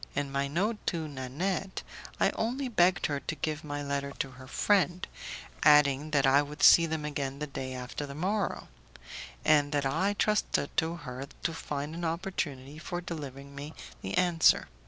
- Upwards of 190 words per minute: No, average, 175 wpm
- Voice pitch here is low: No, medium, 150 Hz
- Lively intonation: No, average, 3.7 semitones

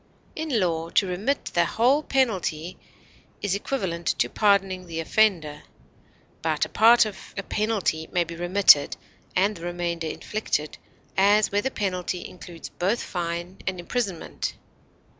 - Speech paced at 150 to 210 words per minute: No, average, 140 wpm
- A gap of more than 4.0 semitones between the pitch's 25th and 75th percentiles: No, average, 3.7 semitones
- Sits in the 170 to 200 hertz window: Yes, medium, 185 Hz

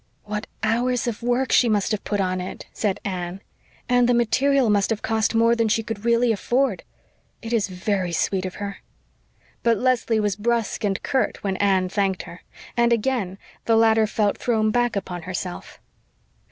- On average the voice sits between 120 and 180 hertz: No, high, 220 Hz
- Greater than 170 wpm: Yes, average, 180 wpm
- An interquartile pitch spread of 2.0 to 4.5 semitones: Yes, average, 3.2 semitones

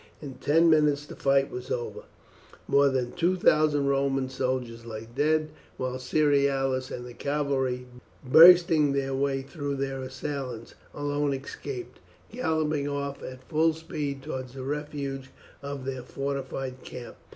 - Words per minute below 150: Yes, average, 140 wpm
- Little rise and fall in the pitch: Yes, narrow, 2.1 semitones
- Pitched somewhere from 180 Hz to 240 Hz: No, medium, 140 Hz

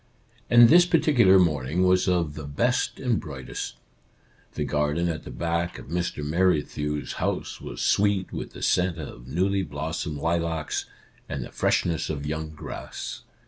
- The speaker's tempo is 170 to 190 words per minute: No, average, 150 wpm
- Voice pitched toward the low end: Yes, very low, 85 Hz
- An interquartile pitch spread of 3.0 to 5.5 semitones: Yes, average, 3.9 semitones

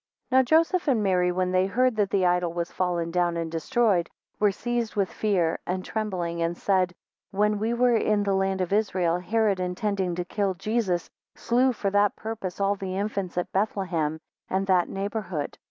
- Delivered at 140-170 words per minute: No, average, 185 wpm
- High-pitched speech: Yes, high, 195 Hz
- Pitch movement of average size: Yes, average, 3.0 semitones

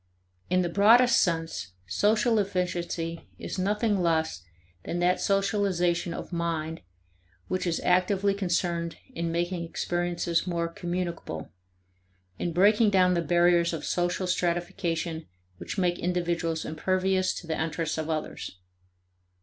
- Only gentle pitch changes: Yes, narrow, 1.9 semitones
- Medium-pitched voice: Yes, medium, 175 Hz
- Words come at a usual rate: No, slow, 125 wpm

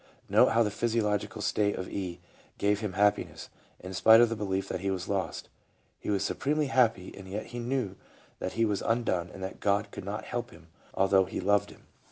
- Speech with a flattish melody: No, average, 3.0 semitones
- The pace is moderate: No, fast, 210 wpm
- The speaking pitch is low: Yes, low, 100 Hz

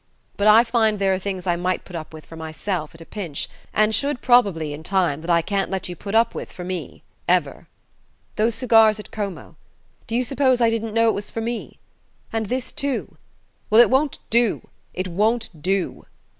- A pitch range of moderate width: Yes, average, 4.4 semitones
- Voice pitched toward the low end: No, high, 210 Hz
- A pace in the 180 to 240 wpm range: Yes, fast, 205 wpm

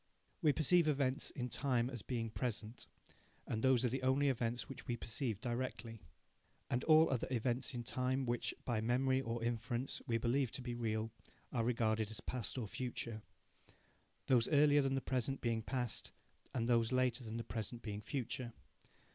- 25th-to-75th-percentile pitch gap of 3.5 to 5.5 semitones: No, narrow, 2.4 semitones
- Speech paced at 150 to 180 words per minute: Yes, average, 170 wpm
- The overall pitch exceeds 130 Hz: No, low, 120 Hz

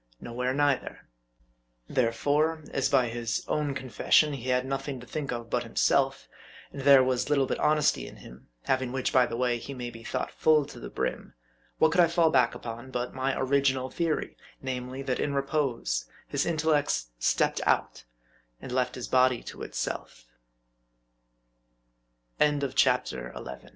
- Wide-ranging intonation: No, narrow, 2.6 semitones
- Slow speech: No, average, 150 wpm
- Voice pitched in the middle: No, low, 130 Hz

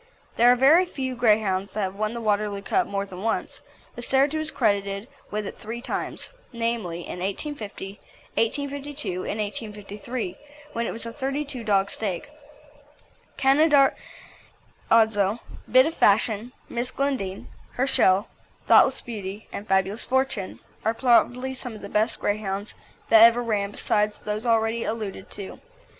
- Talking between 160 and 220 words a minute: No, average, 145 wpm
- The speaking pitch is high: Yes, high, 220 Hz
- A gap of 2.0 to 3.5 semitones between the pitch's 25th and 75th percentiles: No, average, 4.0 semitones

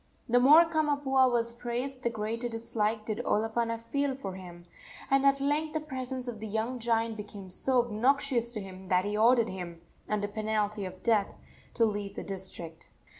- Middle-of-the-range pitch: No, high, 230 Hz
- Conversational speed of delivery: Yes, average, 175 wpm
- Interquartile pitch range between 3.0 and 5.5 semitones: Yes, average, 3.7 semitones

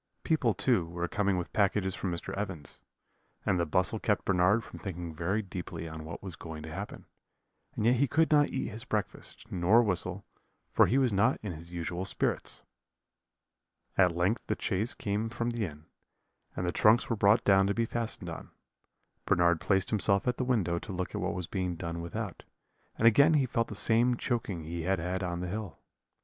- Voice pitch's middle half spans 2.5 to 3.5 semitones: No, average, 4.7 semitones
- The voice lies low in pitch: Yes, very low, 95 Hz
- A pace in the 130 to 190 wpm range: No, average, 200 wpm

